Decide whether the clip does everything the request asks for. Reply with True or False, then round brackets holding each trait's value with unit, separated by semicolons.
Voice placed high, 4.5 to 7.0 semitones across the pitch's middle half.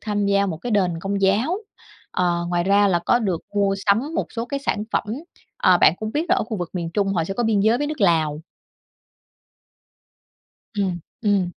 False (200 Hz; 3.7 semitones)